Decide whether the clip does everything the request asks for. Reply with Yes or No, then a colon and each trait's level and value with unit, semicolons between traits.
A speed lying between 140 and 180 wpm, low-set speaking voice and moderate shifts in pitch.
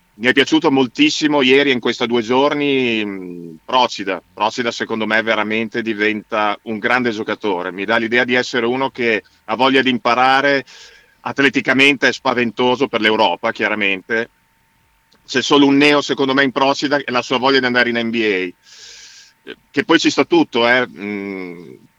Yes: average, 160 wpm; low, 120 Hz; average, 3.6 semitones